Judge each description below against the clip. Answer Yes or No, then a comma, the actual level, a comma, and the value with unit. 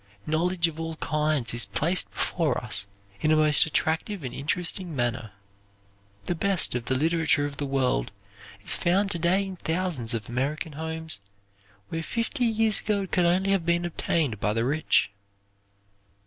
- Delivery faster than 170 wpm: No, average, 165 wpm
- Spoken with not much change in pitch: No, average, 4.5 semitones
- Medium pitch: Yes, medium, 160 Hz